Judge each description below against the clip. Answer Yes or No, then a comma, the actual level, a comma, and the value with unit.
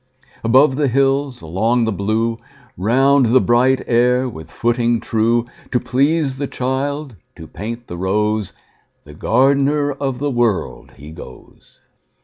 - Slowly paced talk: Yes, slow, 125 wpm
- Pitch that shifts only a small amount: No, average, 3.5 semitones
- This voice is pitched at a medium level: No, low, 120 Hz